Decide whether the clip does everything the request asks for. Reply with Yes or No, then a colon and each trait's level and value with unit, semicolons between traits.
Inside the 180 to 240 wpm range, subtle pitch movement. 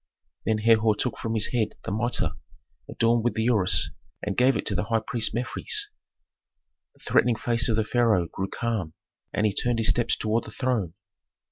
Yes: average, 190 wpm; narrow, 2.0 semitones